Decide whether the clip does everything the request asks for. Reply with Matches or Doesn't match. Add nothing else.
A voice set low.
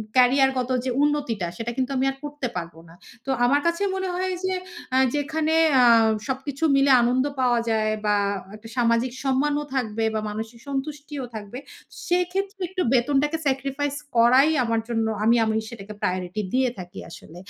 Doesn't match